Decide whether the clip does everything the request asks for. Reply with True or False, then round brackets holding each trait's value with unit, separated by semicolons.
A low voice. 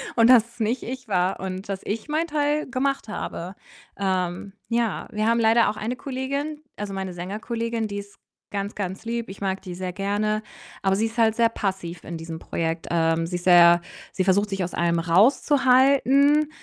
False (210 Hz)